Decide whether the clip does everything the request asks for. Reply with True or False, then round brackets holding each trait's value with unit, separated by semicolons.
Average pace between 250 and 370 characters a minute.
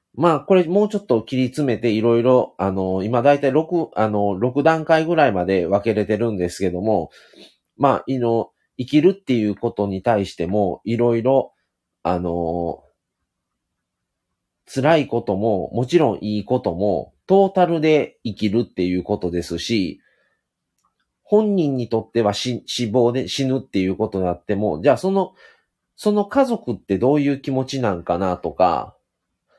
True (310 characters per minute)